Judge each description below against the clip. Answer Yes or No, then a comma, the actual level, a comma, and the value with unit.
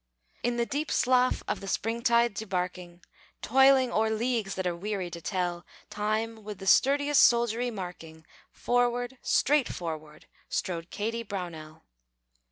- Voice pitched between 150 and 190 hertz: No, high, 215 Hz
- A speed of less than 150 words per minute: Yes, slow, 135 wpm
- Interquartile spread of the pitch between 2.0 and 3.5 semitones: No, average, 5.2 semitones